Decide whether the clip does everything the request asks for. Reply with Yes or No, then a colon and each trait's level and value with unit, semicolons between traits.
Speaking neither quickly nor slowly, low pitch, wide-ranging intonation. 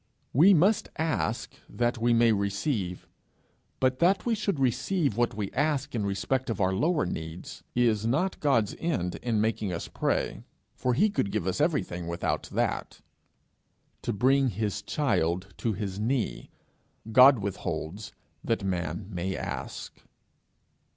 Yes: average, 145 wpm; low, 115 Hz; wide, 6.0 semitones